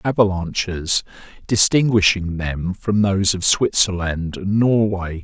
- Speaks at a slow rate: Yes, slow, 105 wpm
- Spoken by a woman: No, male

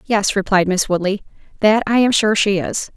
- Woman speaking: Yes, female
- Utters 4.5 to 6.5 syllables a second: Yes, 5.0 syllables/s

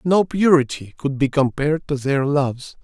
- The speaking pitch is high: No, medium, 145 Hz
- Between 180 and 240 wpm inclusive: No, average, 170 wpm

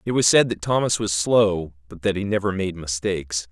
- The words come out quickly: Yes, fast, 220 wpm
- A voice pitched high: No, very low, 95 Hz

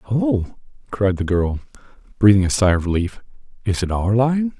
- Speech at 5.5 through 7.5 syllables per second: No, 5.0 syllables/s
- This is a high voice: No, low, 100 Hz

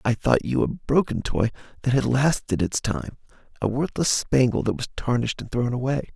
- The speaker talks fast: No, average, 195 wpm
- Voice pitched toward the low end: Yes, low, 125 Hz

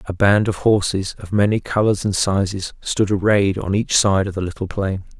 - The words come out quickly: Yes, fast, 210 wpm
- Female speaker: No, male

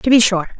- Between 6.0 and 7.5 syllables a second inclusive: Yes, 6.3 syllables/s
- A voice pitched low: No, high, 215 Hz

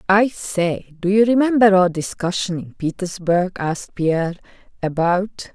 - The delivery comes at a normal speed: No, slow, 130 wpm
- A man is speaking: No, female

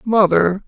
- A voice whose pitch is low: No, high, 200 Hz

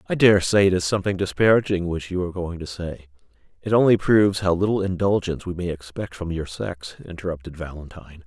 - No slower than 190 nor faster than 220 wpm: Yes, average, 195 wpm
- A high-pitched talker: No, very low, 90 Hz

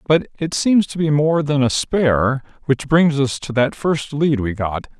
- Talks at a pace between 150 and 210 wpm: Yes, fast, 205 wpm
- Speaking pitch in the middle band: Yes, medium, 145 Hz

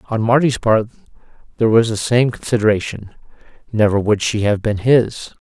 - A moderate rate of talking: Yes, average, 155 wpm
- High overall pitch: No, low, 110 Hz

